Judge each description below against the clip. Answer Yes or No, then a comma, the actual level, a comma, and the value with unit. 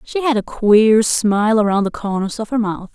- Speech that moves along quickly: Yes, fast, 225 wpm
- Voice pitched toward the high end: Yes, high, 215 Hz